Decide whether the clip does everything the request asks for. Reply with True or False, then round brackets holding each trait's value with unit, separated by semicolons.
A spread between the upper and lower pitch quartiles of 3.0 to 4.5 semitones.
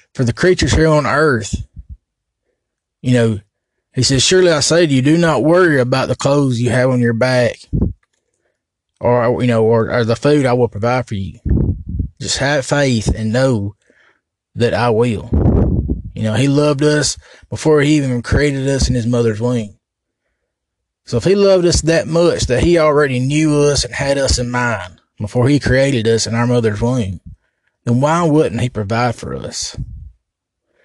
True (4.1 semitones)